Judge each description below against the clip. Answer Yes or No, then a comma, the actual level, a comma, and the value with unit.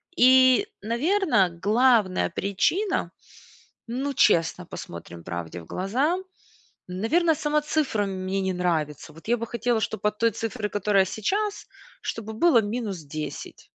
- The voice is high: Yes, high, 220 Hz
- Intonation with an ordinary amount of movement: No, wide, 6.0 semitones